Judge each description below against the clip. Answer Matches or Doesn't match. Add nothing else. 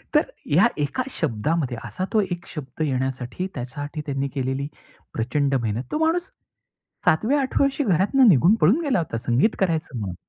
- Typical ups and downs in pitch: Doesn't match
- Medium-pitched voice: Matches